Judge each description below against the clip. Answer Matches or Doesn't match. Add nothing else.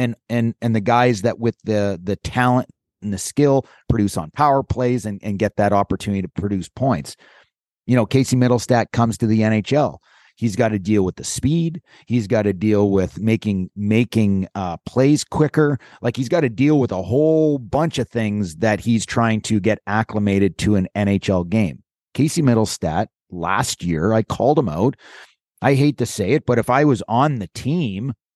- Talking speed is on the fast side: Doesn't match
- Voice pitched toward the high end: Doesn't match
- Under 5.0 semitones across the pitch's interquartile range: Matches